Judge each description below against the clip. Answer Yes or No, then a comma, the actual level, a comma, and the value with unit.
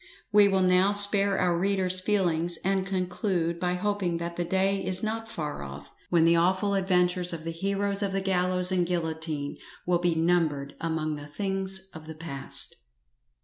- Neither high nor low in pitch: Yes, medium, 180 Hz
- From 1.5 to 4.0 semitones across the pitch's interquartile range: Yes, average, 2.7 semitones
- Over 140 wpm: Yes, average, 175 wpm